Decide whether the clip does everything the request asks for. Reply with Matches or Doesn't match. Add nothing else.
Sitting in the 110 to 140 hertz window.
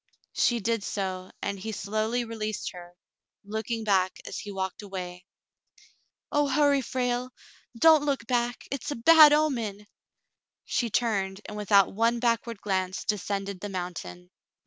Doesn't match